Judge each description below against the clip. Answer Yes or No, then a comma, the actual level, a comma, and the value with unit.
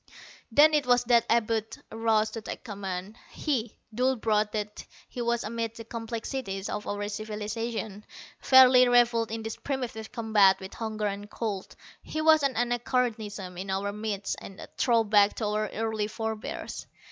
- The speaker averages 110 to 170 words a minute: Yes, average, 155 wpm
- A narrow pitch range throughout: Yes, narrow, 2.2 semitones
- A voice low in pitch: No, high, 220 Hz